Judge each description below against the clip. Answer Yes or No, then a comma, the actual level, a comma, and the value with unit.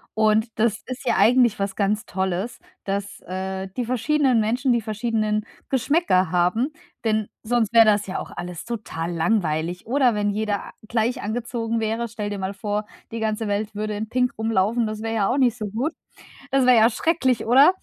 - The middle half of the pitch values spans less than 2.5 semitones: No, average, 2.8 semitones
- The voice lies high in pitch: Yes, high, 220 Hz